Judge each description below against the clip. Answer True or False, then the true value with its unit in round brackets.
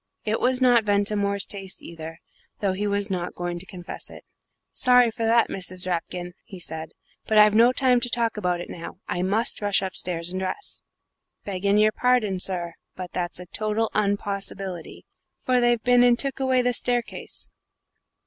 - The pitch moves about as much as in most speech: True (4.5 semitones)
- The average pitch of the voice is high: True (205 Hz)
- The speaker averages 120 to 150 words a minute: False (175 wpm)